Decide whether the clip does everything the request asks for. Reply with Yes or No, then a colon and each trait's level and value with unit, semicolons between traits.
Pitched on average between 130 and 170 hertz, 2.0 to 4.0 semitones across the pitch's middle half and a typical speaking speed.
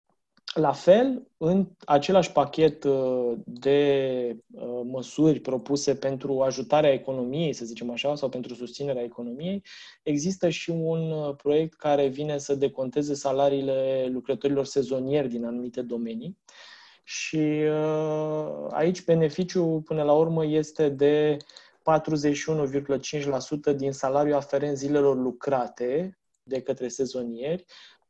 No: medium, 140 Hz; average, 2.7 semitones; slow, 105 wpm